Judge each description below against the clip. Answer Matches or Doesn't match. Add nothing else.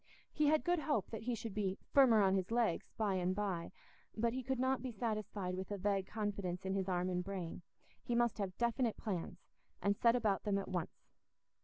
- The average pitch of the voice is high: Matches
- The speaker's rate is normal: Doesn't match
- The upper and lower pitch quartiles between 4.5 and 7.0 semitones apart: Doesn't match